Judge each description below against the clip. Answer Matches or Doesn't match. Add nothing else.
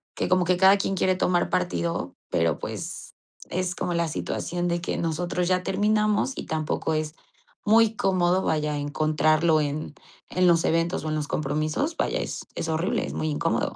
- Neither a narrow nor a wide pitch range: Matches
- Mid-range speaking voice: Matches